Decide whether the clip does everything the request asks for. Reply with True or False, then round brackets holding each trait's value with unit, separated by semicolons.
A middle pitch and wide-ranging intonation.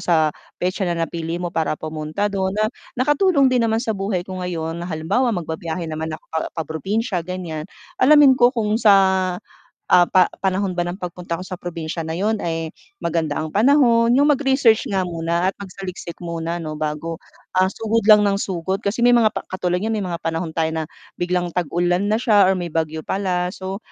False (180 Hz; 4.1 semitones)